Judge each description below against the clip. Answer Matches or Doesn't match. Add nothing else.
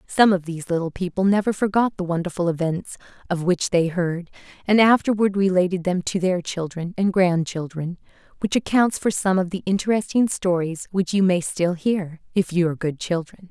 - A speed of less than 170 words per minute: Doesn't match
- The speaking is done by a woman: Matches